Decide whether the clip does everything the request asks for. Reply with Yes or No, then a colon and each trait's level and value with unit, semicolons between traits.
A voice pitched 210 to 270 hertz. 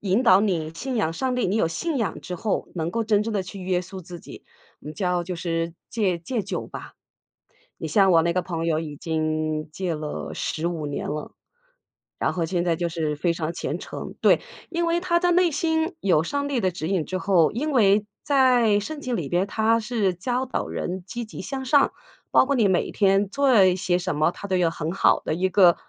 No: medium, 185 Hz